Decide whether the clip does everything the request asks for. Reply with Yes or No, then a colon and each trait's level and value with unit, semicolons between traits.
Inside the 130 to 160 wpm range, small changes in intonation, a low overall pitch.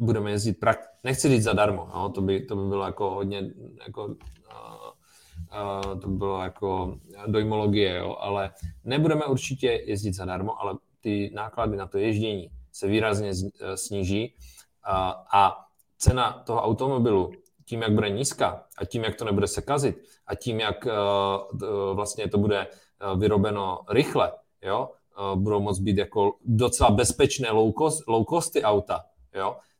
Yes: average, 150 wpm; narrow, 2.2 semitones; low, 105 Hz